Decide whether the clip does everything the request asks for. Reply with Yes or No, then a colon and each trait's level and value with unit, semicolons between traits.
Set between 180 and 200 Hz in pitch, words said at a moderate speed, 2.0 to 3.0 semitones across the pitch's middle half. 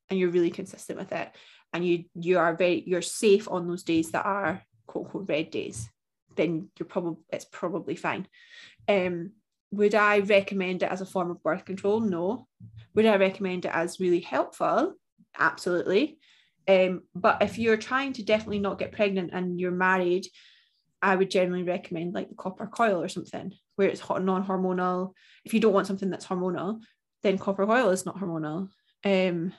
Yes: high, 190 Hz; average, 180 wpm; narrow, 2.6 semitones